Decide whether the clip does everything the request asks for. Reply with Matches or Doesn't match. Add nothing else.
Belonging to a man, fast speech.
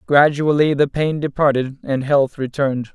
Doesn't match